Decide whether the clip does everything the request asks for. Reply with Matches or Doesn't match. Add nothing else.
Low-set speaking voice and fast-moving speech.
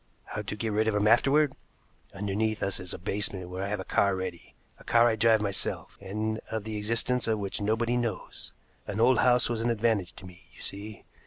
Matches